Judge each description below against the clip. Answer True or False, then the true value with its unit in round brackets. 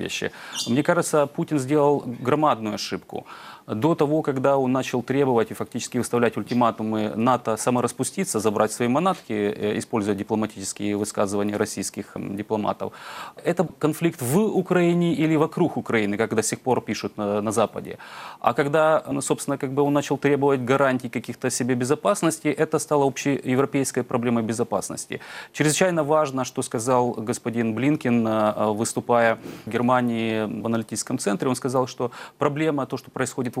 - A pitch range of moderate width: True (4.6 semitones)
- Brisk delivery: False (140 wpm)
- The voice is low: True (125 Hz)